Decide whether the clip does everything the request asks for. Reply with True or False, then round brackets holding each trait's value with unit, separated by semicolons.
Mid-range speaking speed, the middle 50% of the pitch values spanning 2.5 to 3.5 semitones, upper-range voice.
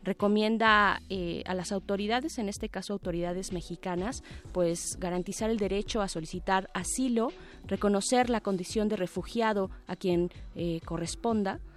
True (135 wpm; 3.0 semitones; 195 Hz)